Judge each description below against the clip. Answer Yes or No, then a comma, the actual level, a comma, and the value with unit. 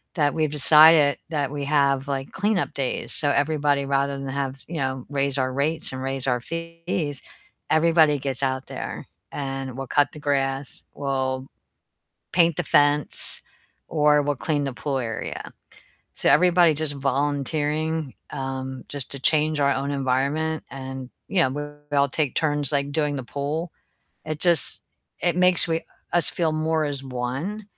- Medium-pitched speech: Yes, medium, 145 Hz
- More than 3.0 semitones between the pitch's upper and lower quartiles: No, narrow, 2.5 semitones